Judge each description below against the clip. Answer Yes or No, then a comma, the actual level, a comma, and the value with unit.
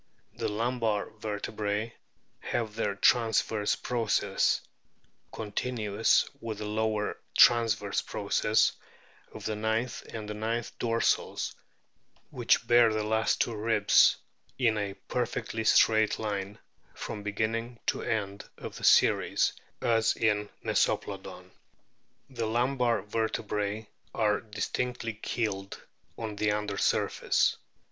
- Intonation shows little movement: Yes, narrow, 1.7 semitones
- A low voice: Yes, low, 110 Hz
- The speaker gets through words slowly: Yes, slow, 110 wpm